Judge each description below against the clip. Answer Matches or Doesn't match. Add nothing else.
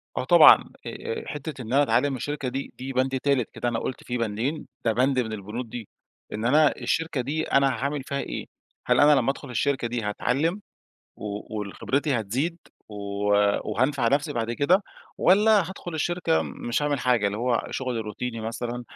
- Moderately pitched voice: Doesn't match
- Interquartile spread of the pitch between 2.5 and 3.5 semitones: Doesn't match